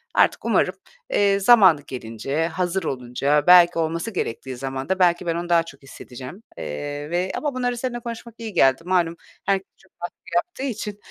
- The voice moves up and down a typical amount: No, wide, 6.0 semitones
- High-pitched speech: No, medium, 175 Hz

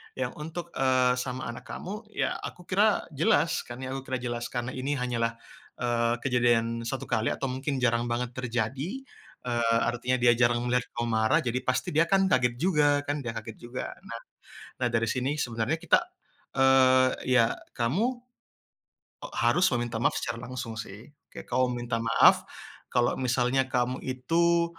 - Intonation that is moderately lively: No, narrow, 2.2 semitones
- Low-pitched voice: Yes, low, 125 Hz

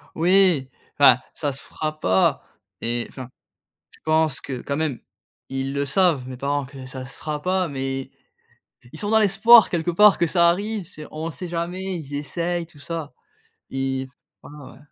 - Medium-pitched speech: Yes, medium, 155 Hz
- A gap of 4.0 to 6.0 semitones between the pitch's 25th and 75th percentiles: Yes, average, 4.7 semitones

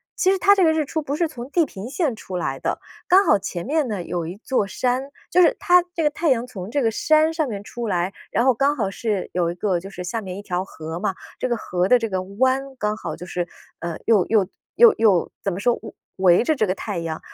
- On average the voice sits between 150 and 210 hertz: No, high, 220 Hz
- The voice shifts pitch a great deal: Yes, wide, 7.4 semitones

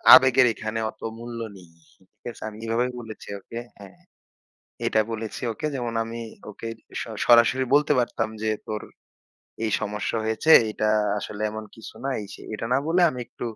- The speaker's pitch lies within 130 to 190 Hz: No, low, 115 Hz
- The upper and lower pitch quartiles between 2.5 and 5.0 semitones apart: No, narrow, 2.1 semitones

